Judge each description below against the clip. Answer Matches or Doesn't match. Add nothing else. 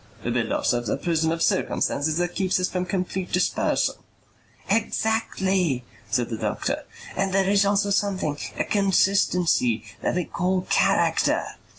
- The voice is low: Doesn't match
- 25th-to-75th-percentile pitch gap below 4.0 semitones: Matches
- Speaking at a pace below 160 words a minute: Matches